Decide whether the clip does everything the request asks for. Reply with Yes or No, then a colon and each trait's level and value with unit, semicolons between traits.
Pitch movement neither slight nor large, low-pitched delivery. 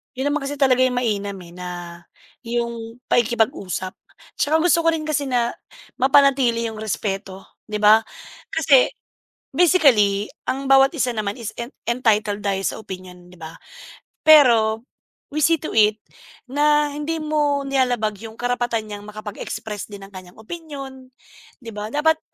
No: average, 4.8 semitones; high, 235 Hz